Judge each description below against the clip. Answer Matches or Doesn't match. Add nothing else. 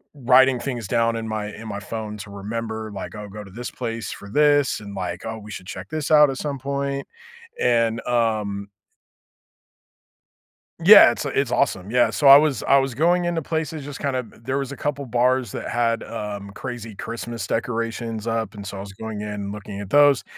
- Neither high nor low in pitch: Doesn't match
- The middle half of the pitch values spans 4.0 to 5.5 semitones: Matches